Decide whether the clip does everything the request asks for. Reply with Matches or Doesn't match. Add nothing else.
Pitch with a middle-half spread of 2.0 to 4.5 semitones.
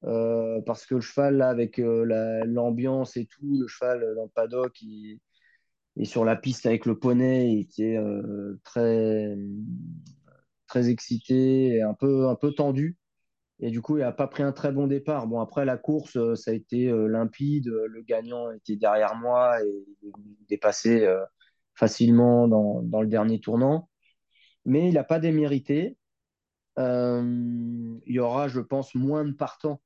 Matches